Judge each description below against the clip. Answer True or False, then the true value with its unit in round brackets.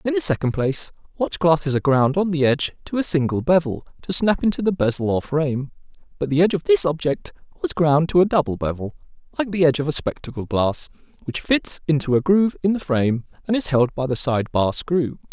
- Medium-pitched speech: True (155 Hz)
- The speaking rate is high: True (225 wpm)